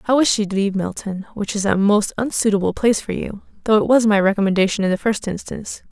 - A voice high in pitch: Yes, high, 205 Hz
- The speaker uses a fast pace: Yes, fast, 225 wpm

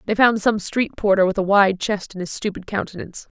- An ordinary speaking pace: No, fast, 230 wpm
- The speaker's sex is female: Yes, female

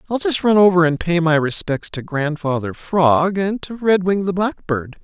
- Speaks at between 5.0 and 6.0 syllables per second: No, 4.6 syllables/s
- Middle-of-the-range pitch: Yes, medium, 175 Hz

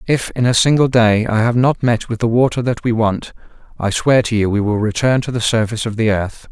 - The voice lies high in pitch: No, low, 115 Hz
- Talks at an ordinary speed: No, fast, 260 wpm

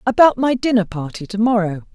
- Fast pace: No, average, 185 wpm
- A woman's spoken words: Yes, female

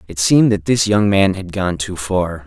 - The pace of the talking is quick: Yes, fast, 245 wpm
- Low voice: Yes, very low, 95 Hz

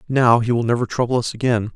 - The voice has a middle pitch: No, low, 120 Hz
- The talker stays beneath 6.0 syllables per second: No, 6.4 syllables/s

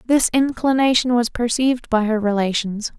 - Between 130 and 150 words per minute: Yes, average, 140 wpm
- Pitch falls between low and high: No, high, 235 Hz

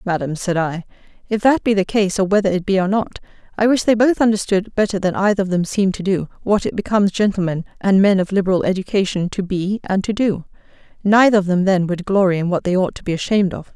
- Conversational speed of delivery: No, fast, 230 wpm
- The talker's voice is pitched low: No, high, 195 Hz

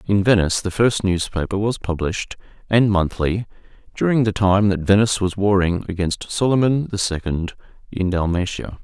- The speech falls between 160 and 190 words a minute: No, average, 150 wpm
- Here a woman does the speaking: No, male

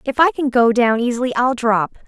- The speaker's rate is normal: No, fast, 230 wpm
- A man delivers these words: No, female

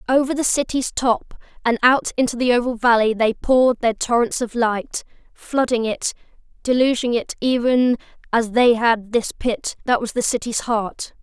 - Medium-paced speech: Yes, average, 165 wpm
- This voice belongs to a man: No, female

